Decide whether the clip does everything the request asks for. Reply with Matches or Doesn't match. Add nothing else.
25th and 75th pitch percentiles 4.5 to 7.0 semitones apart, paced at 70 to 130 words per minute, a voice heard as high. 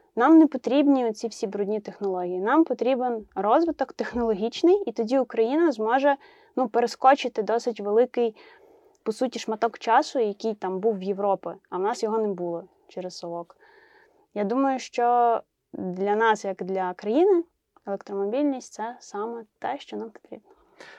Doesn't match